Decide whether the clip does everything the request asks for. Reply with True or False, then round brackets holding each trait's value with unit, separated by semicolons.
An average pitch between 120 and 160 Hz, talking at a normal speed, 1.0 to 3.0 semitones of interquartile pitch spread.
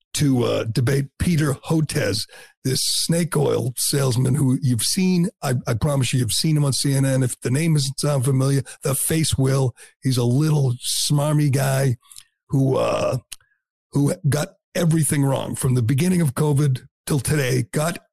True (140 Hz; 155 wpm; 2.6 semitones)